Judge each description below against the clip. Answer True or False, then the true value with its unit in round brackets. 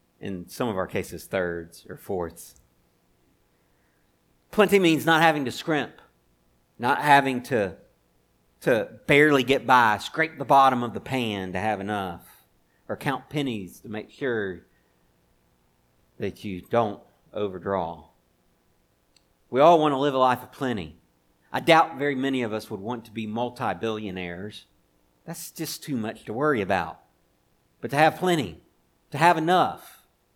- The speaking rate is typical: True (150 wpm)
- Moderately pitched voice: False (100 Hz)